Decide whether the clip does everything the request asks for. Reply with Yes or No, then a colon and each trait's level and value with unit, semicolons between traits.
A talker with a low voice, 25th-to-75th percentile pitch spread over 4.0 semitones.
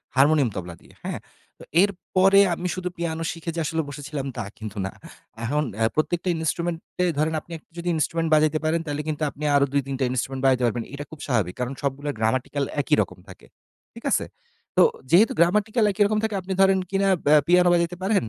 No: medium, 155 Hz; average, 4.4 semitones